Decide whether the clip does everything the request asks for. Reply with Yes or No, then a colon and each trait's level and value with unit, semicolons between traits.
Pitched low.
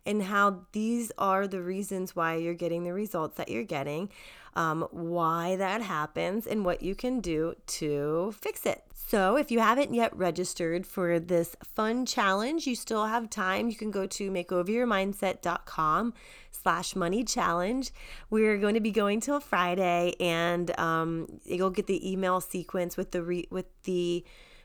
No: medium, 185 Hz